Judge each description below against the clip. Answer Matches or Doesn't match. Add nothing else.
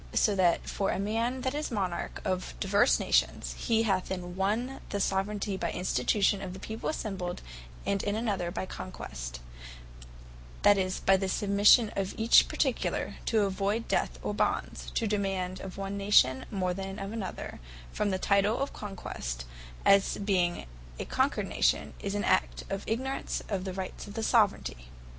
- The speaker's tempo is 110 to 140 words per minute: Doesn't match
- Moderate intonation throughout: Doesn't match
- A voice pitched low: Doesn't match